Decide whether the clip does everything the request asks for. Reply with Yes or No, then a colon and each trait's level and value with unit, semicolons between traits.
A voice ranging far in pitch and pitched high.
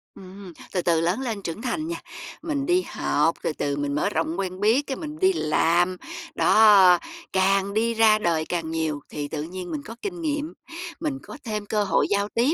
Yes: wide, 6.6 semitones; high, 195 Hz